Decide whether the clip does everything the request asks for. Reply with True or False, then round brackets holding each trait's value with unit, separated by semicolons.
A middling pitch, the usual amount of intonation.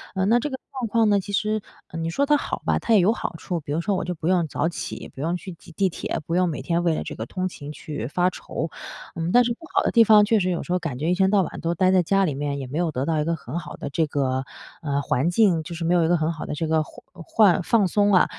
True (175 Hz; 3.8 semitones)